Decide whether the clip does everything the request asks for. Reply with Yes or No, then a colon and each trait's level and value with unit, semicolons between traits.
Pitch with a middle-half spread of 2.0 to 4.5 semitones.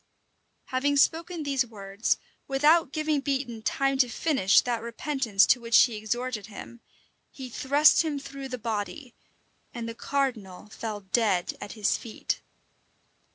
Yes: average, 4.2 semitones